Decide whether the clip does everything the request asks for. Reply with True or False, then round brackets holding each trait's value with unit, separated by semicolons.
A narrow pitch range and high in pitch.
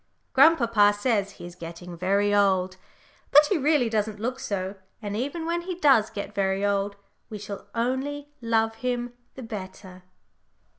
False (4.4 semitones; 215 Hz)